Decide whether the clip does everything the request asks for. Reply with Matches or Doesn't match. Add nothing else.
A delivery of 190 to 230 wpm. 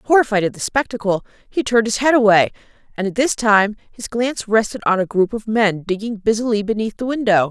Matches